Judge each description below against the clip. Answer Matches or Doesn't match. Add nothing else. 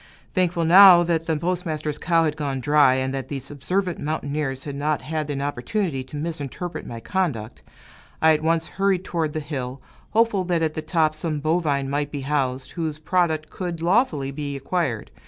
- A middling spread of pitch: Matches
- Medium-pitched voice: Matches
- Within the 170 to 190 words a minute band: Matches